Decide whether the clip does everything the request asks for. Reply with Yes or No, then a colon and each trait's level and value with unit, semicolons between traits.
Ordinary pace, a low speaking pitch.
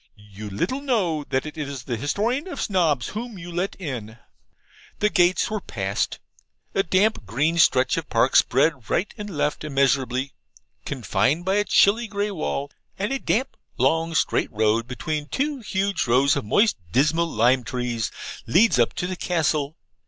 No: average, 165 wpm; medium, 155 Hz